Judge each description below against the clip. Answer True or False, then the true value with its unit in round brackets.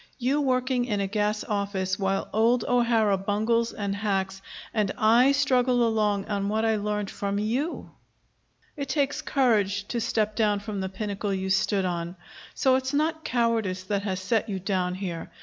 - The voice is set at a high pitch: True (210 Hz)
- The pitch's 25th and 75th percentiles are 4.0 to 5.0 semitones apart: False (3.4 semitones)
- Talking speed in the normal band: True (170 wpm)